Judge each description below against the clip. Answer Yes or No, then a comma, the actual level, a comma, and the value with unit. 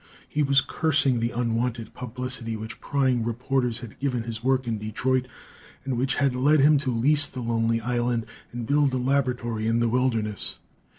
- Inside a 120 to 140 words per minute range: No, average, 175 wpm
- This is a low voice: Yes, low, 125 Hz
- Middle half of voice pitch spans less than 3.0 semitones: Yes, narrow, 2.6 semitones